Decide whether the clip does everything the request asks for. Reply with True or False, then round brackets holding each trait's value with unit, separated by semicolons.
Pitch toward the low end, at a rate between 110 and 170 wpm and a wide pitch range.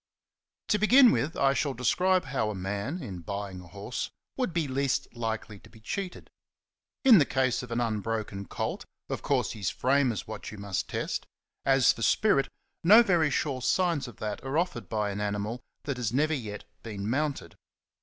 False (125 Hz; 185 wpm; 6.3 semitones)